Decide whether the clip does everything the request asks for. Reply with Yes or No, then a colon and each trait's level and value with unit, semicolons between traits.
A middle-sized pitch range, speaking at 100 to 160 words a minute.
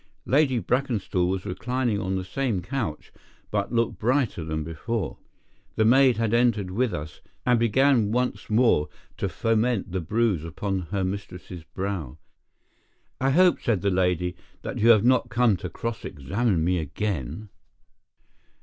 Yes: average, 4.9 semitones; average, 150 wpm